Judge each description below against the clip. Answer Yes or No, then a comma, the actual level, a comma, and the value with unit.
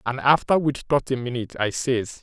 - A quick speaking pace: Yes, fast, 215 wpm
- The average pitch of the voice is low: Yes, low, 125 Hz